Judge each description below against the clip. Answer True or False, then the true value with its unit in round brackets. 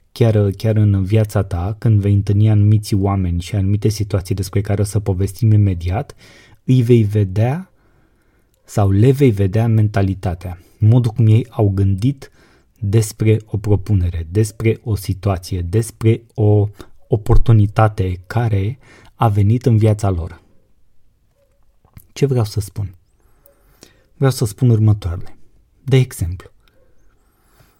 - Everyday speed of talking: True (125 wpm)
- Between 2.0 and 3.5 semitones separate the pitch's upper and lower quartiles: True (2.5 semitones)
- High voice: False (105 Hz)